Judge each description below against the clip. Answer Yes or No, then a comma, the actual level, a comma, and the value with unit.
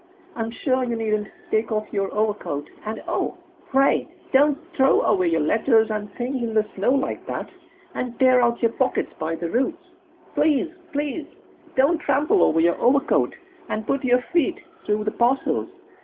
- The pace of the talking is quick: No, average, 170 wpm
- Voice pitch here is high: Yes, high, 240 Hz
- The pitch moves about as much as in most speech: Yes, average, 4.2 semitones